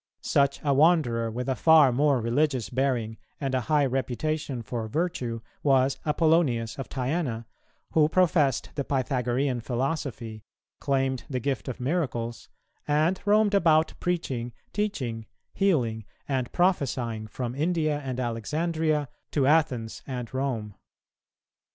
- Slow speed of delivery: Yes, slow, 125 wpm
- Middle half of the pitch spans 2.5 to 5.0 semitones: Yes, average, 4.4 semitones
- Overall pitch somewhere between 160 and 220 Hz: No, low, 135 Hz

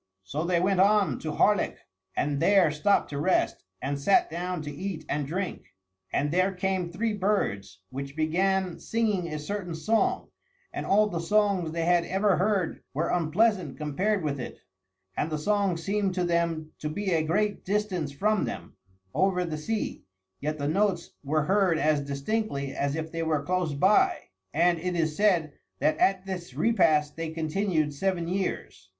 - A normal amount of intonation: Yes, average, 4.2 semitones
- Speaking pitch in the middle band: Yes, medium, 170 Hz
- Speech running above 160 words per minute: Yes, average, 175 wpm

